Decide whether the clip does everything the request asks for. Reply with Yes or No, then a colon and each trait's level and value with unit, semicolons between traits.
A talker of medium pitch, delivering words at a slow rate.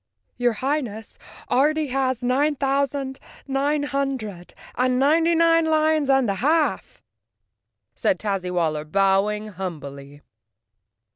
No: very high, 260 Hz; slow, 120 wpm